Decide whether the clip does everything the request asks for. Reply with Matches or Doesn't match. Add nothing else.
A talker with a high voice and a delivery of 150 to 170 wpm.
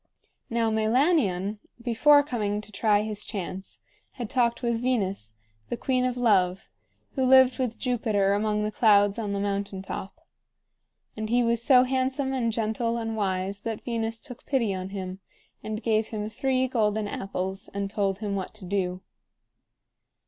Matches